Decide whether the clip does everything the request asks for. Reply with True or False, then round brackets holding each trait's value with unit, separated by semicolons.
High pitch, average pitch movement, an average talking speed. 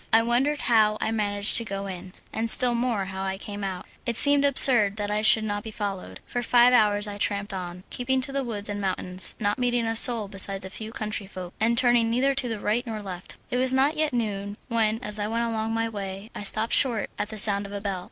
False (215 Hz; 3.0 semitones; 240 wpm)